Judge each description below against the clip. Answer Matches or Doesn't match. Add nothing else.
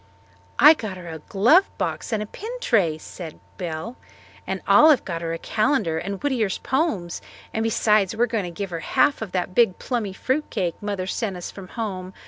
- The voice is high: Matches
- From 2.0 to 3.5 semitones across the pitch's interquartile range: Doesn't match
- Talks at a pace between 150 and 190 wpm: Doesn't match